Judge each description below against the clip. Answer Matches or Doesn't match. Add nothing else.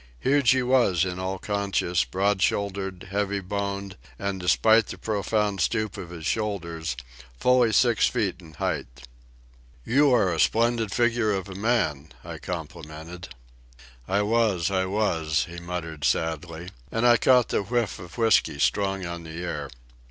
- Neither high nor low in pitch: Doesn't match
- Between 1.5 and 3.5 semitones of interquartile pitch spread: Doesn't match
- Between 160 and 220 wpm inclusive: Doesn't match